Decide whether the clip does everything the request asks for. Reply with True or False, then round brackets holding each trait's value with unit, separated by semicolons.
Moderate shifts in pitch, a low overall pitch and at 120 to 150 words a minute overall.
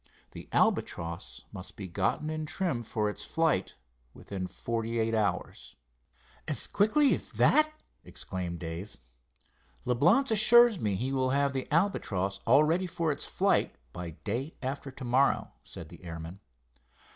False (8.6 semitones; 125 Hz; 145 wpm)